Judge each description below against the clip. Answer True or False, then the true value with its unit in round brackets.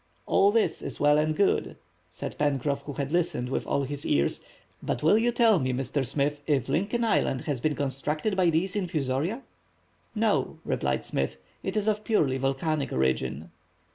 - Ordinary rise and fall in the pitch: False (6.2 semitones)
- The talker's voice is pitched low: False (150 Hz)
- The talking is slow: False (170 wpm)